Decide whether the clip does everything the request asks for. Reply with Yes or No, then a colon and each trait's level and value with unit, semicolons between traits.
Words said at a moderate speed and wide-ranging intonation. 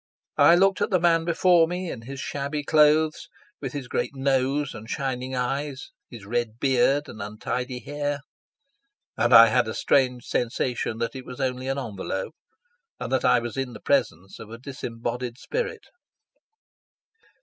No: average, 160 wpm; average, 3.5 semitones